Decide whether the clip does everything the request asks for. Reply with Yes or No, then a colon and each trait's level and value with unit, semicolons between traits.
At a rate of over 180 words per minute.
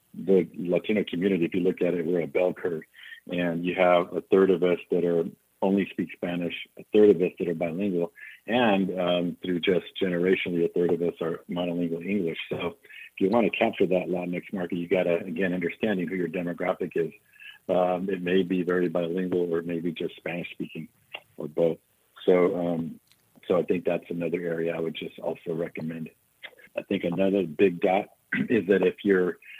Yes: average, 195 wpm